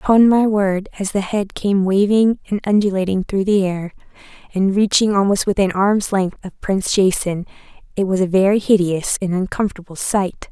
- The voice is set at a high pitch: Yes, high, 195 Hz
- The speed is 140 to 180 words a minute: Yes, average, 170 wpm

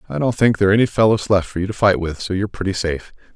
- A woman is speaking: No, male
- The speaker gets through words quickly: Yes, fast, 285 wpm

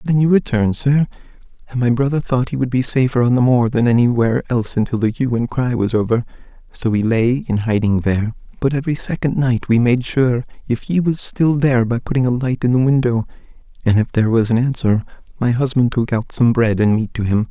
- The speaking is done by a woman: No, male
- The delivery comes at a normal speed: No, fast, 225 wpm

